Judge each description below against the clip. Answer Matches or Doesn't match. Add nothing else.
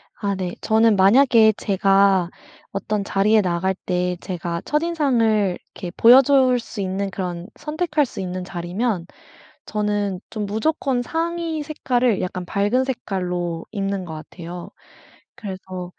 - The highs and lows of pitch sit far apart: Doesn't match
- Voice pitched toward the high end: Matches